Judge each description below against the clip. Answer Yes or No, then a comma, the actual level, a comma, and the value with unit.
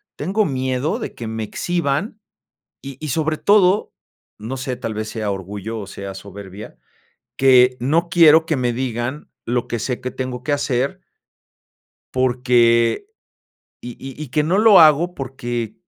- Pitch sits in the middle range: No, low, 130 Hz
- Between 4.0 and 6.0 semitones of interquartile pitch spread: Yes, average, 4.6 semitones